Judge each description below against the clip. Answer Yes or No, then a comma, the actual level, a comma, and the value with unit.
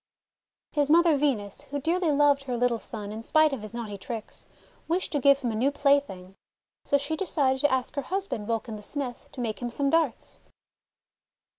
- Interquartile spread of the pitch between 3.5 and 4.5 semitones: Yes, average, 4.1 semitones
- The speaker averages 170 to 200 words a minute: Yes, average, 190 wpm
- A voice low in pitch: No, very high, 275 Hz